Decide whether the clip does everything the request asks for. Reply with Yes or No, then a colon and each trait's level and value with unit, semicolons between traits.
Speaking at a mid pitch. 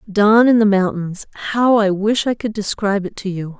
No: high, 205 Hz